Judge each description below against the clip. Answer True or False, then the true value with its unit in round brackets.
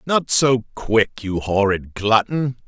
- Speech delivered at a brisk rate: False (135 wpm)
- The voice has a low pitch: True (115 Hz)